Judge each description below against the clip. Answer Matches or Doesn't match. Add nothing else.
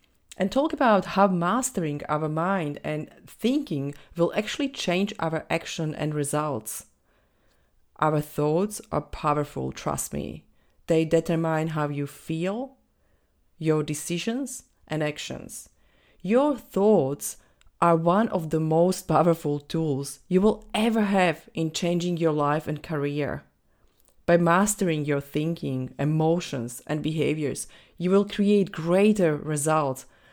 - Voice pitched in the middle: Matches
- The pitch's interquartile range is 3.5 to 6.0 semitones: Matches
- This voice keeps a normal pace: Doesn't match